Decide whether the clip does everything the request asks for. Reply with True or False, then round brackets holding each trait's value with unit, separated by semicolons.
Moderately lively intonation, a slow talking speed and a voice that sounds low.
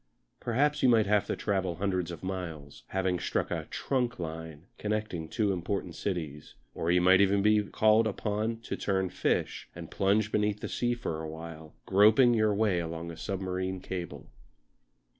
False (3.7 semitones; 170 wpm; 95 Hz)